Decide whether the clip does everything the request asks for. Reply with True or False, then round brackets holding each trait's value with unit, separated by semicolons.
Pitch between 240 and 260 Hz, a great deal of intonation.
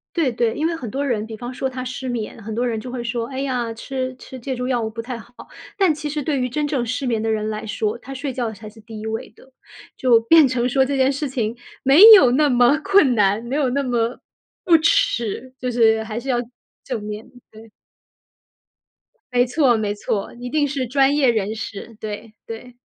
False (245 Hz; 3.2 semitones)